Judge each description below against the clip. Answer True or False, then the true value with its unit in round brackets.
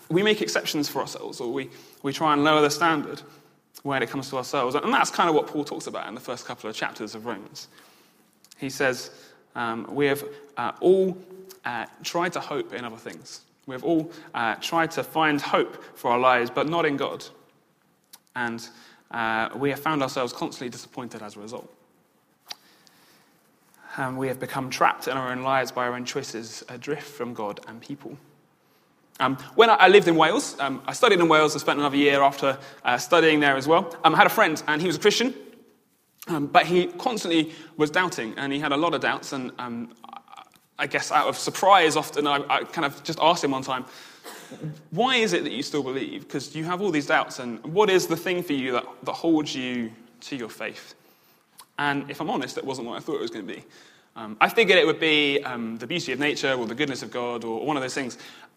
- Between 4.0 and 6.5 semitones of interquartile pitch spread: True (4.5 semitones)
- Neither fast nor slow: False (220 wpm)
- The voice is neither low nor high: True (145 Hz)